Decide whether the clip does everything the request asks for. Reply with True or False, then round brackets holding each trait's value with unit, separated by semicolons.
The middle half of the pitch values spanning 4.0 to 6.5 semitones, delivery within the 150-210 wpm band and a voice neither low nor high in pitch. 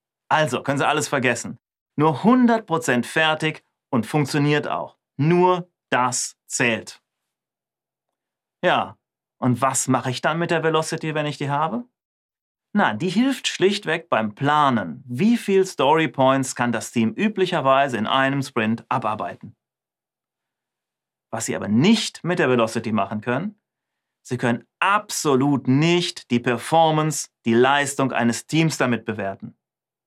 False (5.0 semitones; 130 wpm; 145 Hz)